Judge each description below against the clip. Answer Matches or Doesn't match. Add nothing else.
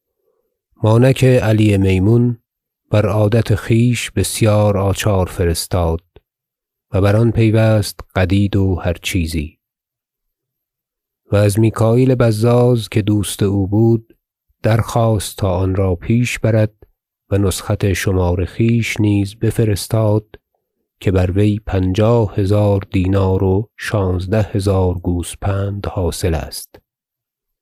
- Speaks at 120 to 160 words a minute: Doesn't match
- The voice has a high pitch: Doesn't match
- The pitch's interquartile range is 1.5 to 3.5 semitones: Matches